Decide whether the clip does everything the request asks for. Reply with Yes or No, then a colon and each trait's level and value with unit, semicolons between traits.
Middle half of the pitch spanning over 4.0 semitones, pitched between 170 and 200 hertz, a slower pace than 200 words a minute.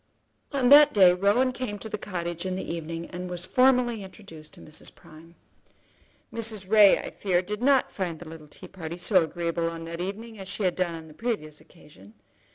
No: average, 4.4 semitones; medium, 185 Hz; fast, 205 wpm